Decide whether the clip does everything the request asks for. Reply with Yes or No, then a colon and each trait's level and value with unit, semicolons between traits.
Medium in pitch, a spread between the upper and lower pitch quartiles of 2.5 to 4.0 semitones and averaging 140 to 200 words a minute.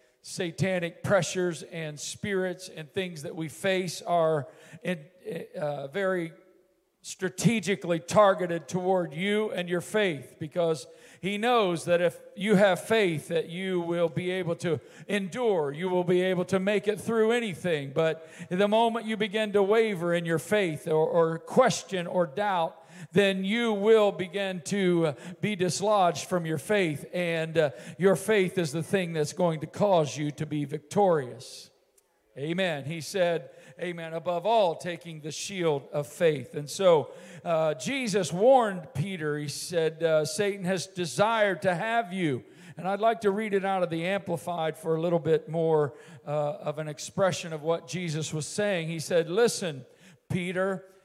Yes: medium, 175 Hz; average, 3.3 semitones; average, 160 wpm